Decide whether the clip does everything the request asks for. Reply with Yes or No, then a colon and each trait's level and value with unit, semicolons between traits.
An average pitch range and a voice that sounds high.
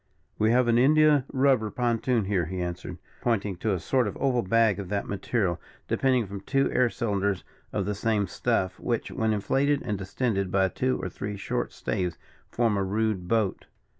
No: average, 4.0 semitones; low, 105 Hz